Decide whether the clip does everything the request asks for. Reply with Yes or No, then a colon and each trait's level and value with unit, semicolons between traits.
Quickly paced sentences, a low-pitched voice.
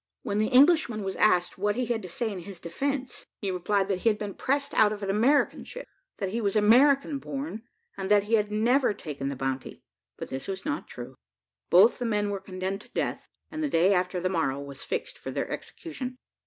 No: fast, 220 wpm; high, 205 Hz